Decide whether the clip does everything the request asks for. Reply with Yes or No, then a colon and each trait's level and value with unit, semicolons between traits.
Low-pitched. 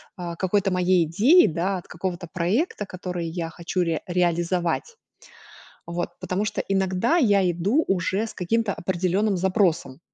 No: medium, 185 Hz